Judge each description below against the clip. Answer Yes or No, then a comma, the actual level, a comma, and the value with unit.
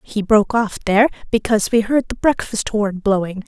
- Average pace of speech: Yes, average, 190 wpm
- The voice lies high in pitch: Yes, high, 215 Hz